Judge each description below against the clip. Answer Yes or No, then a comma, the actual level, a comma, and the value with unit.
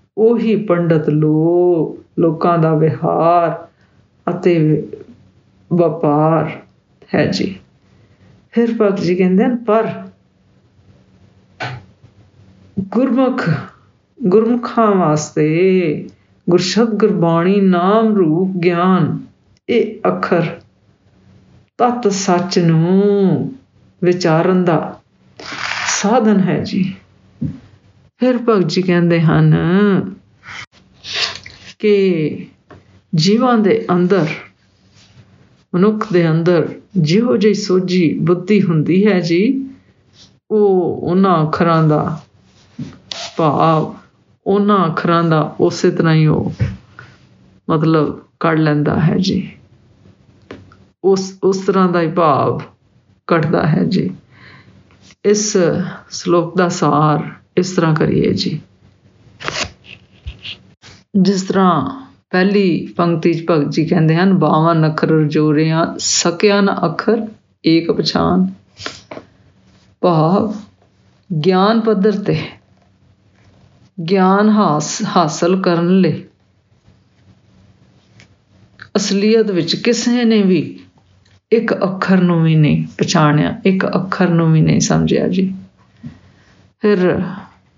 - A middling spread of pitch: Yes, average, 4.6 semitones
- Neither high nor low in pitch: Yes, medium, 175 Hz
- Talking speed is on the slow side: Yes, slow, 85 wpm